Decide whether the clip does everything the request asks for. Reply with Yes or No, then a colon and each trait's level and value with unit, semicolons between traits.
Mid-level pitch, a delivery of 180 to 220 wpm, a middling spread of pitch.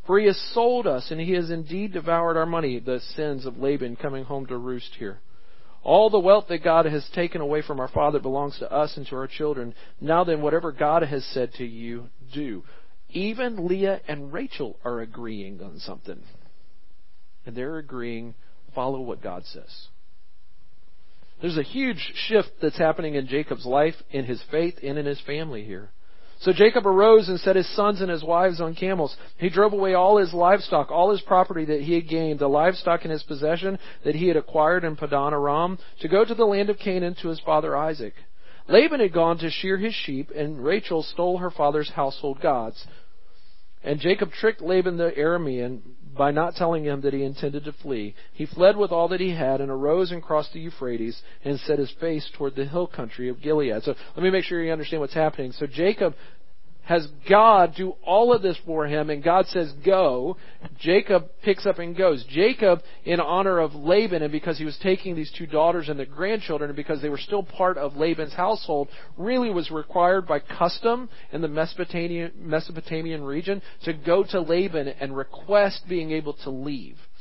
Yes: medium, 160 Hz; average, 195 wpm; average, 4.2 semitones